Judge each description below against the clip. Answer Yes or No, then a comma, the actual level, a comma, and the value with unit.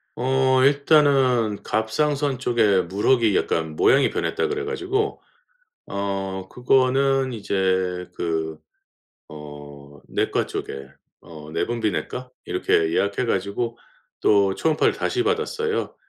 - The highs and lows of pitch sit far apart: Yes, wide, 6.6 semitones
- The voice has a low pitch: Yes, low, 115 Hz